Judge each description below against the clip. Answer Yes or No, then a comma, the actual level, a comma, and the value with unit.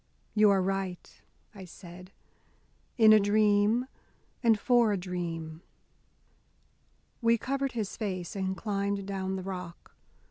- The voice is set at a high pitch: Yes, high, 200 Hz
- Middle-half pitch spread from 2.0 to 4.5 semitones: Yes, average, 2.8 semitones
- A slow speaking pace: Yes, slow, 120 wpm